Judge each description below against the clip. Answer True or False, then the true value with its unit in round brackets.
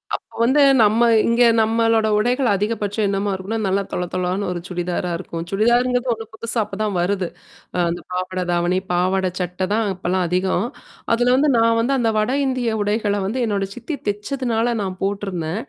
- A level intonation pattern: False (3.7 semitones)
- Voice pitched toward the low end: False (205 Hz)